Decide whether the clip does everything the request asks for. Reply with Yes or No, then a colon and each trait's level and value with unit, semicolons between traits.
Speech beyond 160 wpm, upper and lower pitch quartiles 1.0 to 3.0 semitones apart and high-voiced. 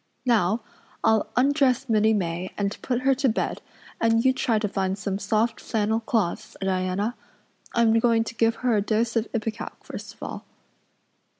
Yes: average, 170 wpm; narrow, 2.4 semitones; high, 225 Hz